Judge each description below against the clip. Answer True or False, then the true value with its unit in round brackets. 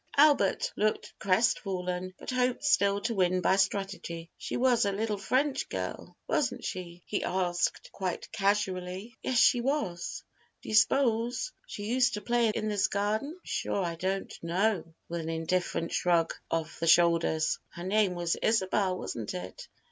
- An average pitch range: True (4.3 semitones)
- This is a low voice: False (195 Hz)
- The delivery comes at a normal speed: True (160 wpm)